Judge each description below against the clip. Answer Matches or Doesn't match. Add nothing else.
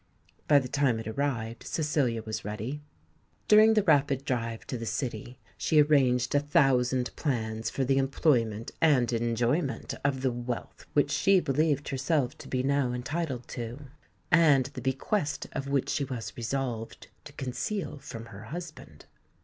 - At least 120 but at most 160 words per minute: Matches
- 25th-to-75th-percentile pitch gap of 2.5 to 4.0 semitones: Matches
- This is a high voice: Doesn't match